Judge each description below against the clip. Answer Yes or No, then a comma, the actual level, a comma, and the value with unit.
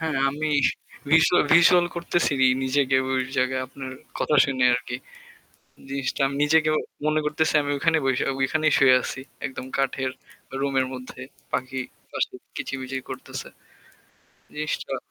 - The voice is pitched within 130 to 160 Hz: Yes, low, 135 Hz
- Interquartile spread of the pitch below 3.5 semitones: Yes, average, 2.9 semitones